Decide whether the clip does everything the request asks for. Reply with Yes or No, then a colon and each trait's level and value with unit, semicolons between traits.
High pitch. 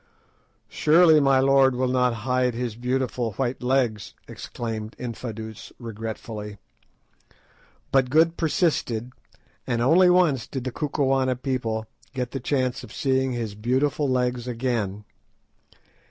No: low, 125 Hz